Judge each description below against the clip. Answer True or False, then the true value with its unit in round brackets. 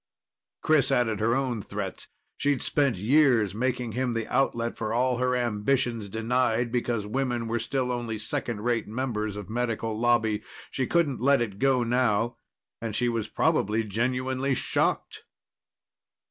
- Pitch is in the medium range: False (120 Hz)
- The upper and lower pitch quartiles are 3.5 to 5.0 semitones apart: False (2.5 semitones)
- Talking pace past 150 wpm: False (145 wpm)